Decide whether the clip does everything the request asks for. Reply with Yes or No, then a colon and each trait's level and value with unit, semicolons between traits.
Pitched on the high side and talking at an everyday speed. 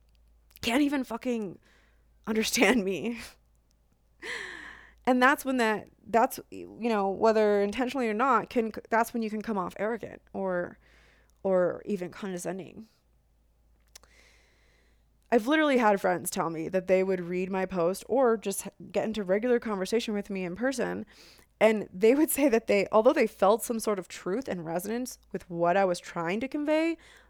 Yes: high, 205 Hz; average, 160 wpm